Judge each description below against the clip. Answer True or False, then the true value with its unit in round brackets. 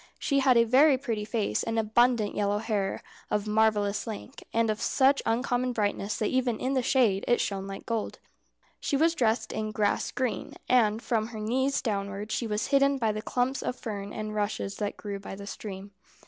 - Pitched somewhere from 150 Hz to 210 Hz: False (220 Hz)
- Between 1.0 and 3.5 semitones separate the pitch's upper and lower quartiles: True (3.2 semitones)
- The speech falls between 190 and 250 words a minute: True (195 wpm)